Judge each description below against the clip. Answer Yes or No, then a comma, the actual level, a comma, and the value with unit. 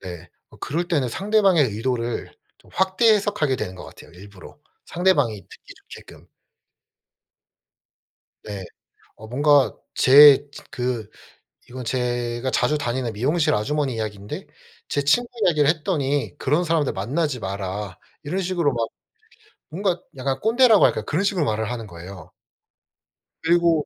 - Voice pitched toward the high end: No, medium, 140 Hz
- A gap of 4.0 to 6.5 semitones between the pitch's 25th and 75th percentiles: No, wide, 6.9 semitones